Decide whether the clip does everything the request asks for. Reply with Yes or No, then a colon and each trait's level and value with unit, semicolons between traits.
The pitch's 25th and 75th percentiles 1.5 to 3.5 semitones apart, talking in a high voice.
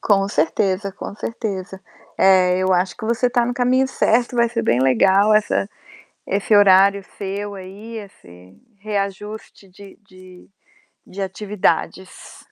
Yes: narrow, 2.4 semitones; high, 200 Hz